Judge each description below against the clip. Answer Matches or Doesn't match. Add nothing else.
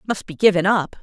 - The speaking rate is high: Matches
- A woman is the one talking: Matches